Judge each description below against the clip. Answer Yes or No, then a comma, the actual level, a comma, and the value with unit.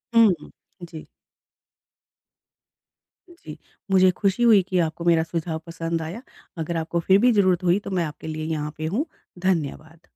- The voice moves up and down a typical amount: Yes, average, 3.0 semitones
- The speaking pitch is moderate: Yes, medium, 170 Hz